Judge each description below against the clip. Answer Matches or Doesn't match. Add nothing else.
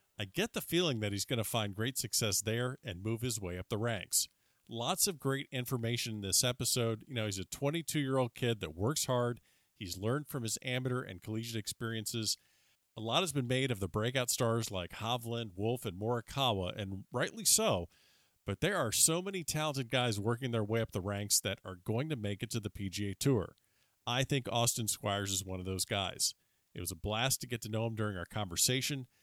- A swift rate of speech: Matches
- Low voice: Matches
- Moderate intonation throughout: Matches